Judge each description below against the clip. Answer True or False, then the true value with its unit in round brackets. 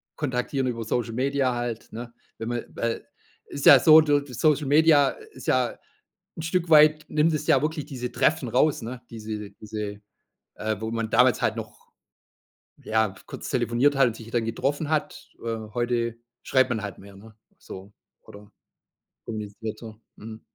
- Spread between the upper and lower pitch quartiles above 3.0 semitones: True (4.5 semitones)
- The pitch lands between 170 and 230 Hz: False (120 Hz)